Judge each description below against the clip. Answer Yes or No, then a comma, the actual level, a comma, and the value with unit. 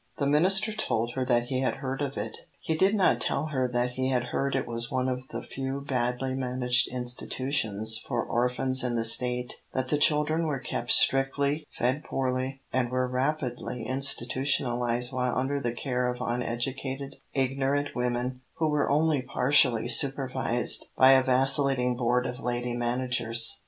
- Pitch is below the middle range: Yes, low, 130 Hz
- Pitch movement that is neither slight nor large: No, narrow, 1.9 semitones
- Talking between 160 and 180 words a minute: Yes, average, 165 wpm